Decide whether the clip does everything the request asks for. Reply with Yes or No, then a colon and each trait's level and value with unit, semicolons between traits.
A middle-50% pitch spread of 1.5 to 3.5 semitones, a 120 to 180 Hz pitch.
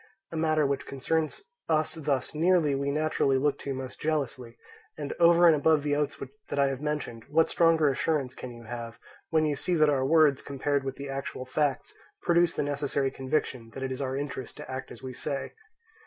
Yes: average, 2.8 semitones; medium, 140 Hz